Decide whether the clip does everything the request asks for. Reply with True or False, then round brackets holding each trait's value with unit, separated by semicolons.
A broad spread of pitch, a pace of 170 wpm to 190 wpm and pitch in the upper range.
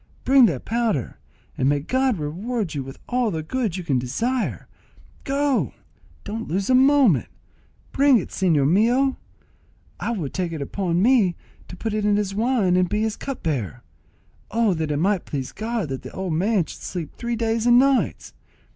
True (6.7 semitones; 180 wpm; 205 Hz)